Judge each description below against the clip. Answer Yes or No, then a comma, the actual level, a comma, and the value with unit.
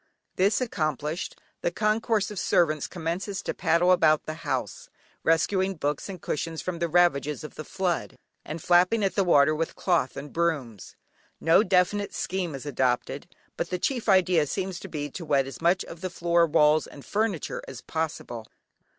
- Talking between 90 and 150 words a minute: No, average, 175 wpm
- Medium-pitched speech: Yes, medium, 170 Hz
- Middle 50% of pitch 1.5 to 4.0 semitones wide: Yes, average, 3.6 semitones